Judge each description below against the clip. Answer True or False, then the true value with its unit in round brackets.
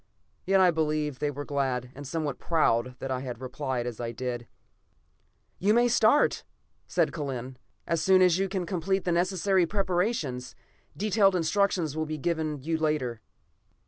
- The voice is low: False (155 Hz)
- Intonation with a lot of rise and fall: True (6.0 semitones)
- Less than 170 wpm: True (160 wpm)